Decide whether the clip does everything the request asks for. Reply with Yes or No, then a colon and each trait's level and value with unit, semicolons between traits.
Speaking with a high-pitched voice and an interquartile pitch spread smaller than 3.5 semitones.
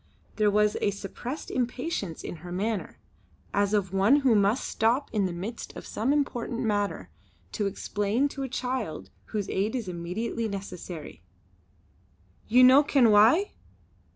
No: high, 215 Hz; average, 4.0 semitones